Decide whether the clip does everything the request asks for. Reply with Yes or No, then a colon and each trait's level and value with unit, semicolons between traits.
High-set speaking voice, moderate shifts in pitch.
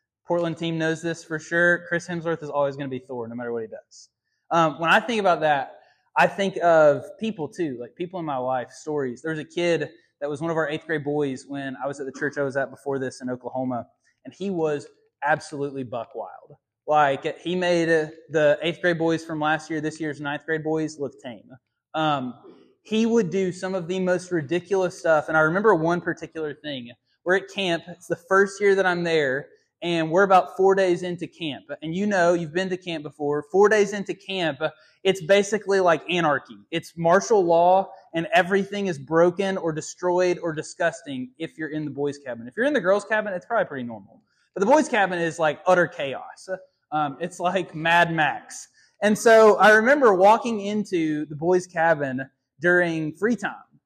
No: medium, 165 Hz; average, 3.7 semitones